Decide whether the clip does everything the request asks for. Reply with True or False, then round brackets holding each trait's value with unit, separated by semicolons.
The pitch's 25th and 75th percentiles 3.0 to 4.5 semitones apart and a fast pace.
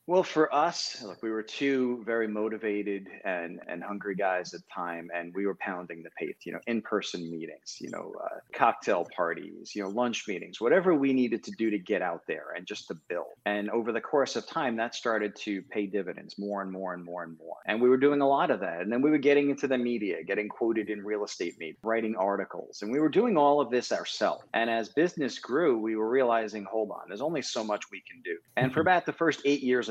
True (4.2 semitones; 245 wpm)